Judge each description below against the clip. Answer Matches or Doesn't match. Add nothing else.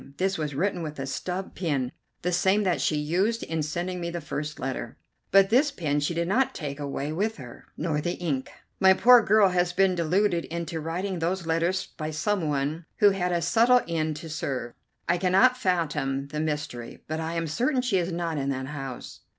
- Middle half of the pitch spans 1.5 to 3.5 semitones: Doesn't match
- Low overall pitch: Doesn't match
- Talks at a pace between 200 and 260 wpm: Matches